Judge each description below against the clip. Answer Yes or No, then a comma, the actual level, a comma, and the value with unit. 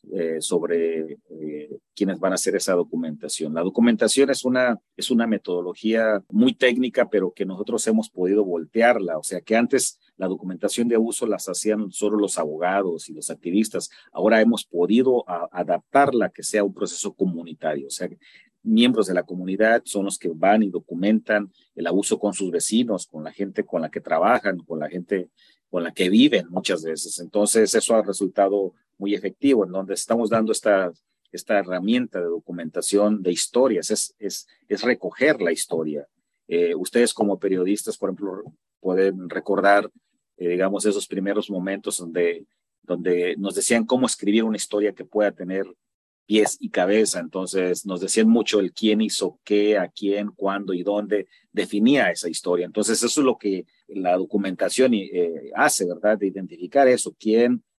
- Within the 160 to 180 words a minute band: Yes, average, 170 wpm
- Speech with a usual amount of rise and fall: Yes, average, 3.5 semitones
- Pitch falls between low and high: No, low, 100 Hz